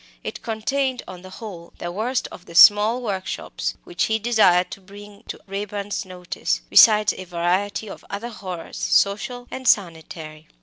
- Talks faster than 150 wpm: Yes, average, 160 wpm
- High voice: Yes, high, 200 Hz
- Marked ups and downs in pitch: No, average, 3.5 semitones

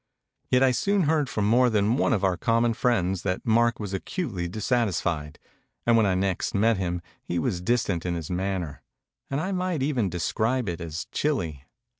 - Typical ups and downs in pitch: No, wide, 5.8 semitones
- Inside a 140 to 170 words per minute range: No, average, 185 wpm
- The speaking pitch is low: Yes, low, 105 Hz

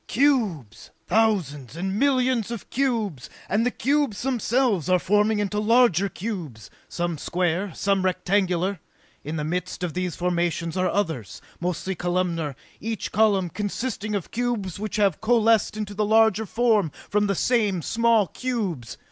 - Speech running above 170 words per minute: No, average, 145 wpm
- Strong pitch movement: No, average, 4.1 semitones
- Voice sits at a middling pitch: No, high, 200 Hz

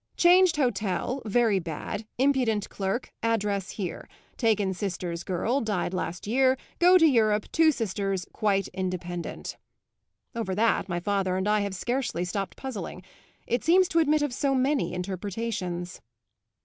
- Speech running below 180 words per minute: Yes, average, 140 wpm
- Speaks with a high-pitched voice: Yes, high, 210 Hz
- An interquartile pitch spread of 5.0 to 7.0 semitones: Yes, wide, 5.5 semitones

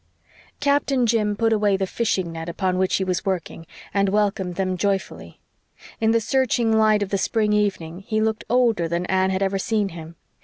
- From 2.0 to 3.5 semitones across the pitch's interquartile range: Yes, average, 2.9 semitones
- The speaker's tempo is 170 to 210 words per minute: Yes, average, 190 wpm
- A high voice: Yes, high, 200 Hz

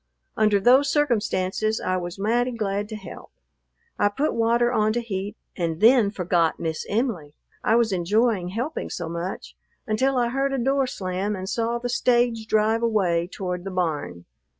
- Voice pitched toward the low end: No, high, 215 Hz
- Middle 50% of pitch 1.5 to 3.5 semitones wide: No, average, 4.5 semitones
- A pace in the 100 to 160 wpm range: No, average, 170 wpm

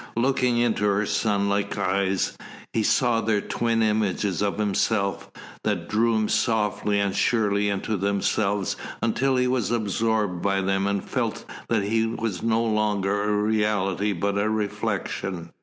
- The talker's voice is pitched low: Yes, low, 105 Hz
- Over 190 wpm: No, average, 145 wpm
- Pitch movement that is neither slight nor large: No, narrow, 2.1 semitones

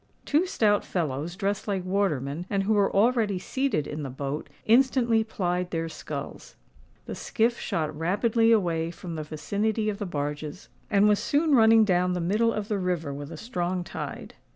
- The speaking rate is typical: Yes, average, 175 wpm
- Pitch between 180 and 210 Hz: Yes, high, 190 Hz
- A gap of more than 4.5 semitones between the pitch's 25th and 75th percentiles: Yes, average, 5.2 semitones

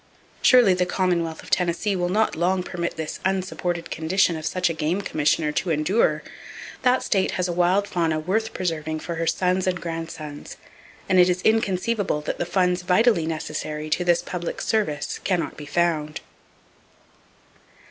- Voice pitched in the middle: Yes, medium, 175 Hz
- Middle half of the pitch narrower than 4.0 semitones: Yes, narrow, 2.6 semitones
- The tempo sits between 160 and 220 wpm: Yes, average, 165 wpm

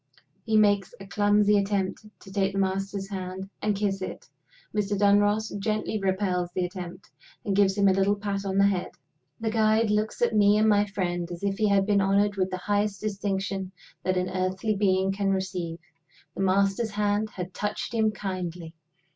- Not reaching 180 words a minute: No, average, 185 wpm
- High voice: Yes, high, 200 Hz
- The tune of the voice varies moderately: No, narrow, 1.6 semitones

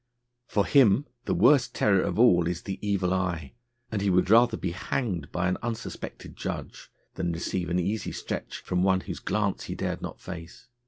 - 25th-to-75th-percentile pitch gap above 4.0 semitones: No, average, 3.2 semitones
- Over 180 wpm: Yes, average, 190 wpm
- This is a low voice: Yes, very low, 95 Hz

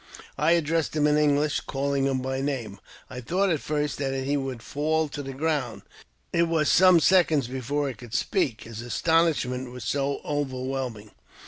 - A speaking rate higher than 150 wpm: Yes, average, 180 wpm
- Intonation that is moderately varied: Yes, average, 3.0 semitones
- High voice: No, medium, 140 Hz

